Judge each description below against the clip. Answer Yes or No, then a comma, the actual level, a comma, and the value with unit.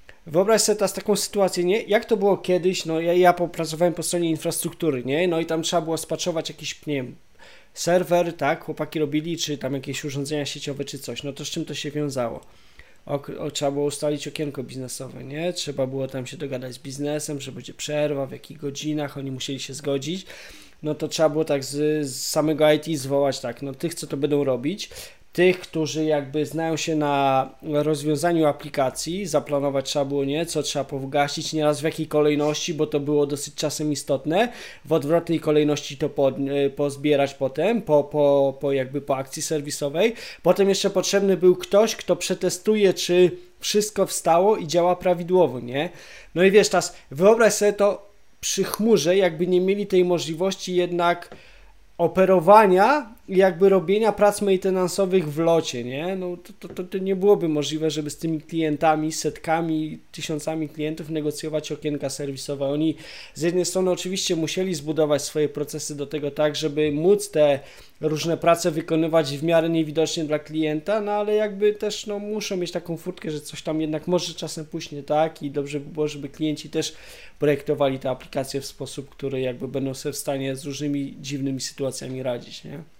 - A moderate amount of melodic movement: Yes, average, 3.6 semitones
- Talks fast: Yes, fast, 175 wpm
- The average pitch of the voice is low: No, medium, 155 Hz